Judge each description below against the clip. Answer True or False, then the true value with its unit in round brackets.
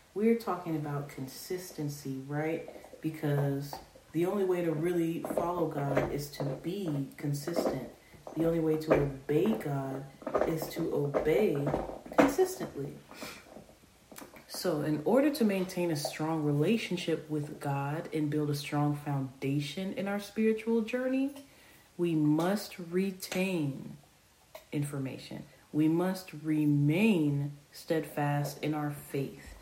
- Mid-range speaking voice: True (155 Hz)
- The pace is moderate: False (115 wpm)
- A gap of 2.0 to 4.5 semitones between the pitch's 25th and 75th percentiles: True (3.9 semitones)